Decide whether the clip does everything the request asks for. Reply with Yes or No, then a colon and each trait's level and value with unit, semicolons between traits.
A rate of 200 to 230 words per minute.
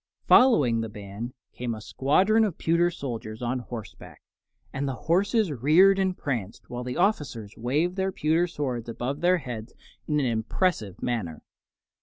No: average, 155 wpm